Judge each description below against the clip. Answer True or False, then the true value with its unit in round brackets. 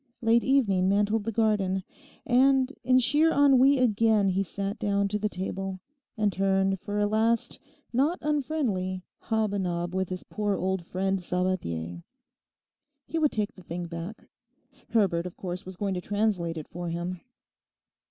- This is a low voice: False (200 Hz)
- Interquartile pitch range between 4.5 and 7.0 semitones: False (3.6 semitones)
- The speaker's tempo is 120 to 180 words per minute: True (160 wpm)